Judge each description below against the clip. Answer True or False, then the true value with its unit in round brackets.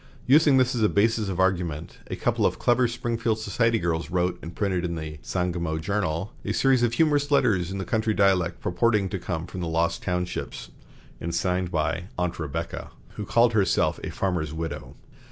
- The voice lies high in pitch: False (90 Hz)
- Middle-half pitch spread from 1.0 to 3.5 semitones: False (4.9 semitones)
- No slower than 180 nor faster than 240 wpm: True (185 wpm)